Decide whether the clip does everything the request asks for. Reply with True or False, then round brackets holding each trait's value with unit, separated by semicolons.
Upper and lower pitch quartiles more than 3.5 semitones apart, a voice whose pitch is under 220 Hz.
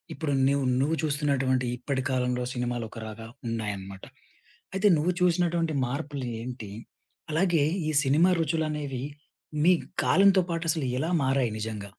True (4.9 semitones; 140 Hz)